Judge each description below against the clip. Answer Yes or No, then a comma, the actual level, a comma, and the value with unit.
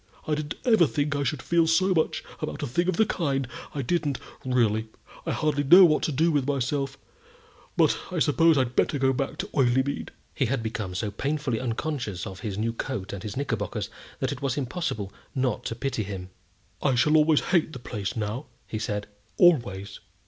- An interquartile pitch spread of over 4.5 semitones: Yes, average, 5.3 semitones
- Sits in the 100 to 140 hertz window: Yes, low, 135 Hz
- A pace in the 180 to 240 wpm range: Yes, average, 195 wpm